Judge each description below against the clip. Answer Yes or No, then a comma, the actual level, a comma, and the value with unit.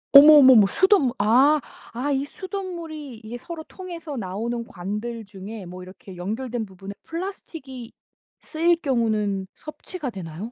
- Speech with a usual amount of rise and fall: No, wide, 7.2 semitones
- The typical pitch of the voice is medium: No, high, 240 Hz